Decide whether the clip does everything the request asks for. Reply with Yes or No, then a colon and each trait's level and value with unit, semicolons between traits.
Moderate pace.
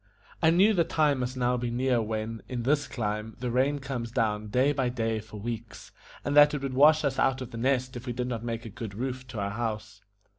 No: fast, 245 wpm